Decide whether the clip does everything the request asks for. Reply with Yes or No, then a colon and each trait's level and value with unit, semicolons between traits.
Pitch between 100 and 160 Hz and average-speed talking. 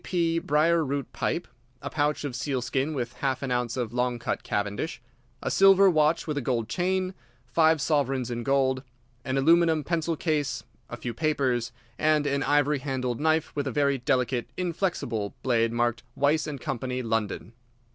Yes: medium, 140 Hz; average, 170 wpm